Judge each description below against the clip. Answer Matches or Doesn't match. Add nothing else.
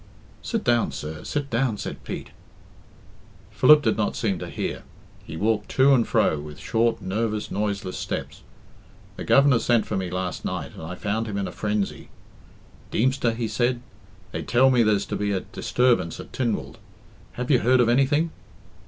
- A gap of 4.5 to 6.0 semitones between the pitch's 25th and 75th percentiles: Doesn't match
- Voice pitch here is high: Doesn't match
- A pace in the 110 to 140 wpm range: Doesn't match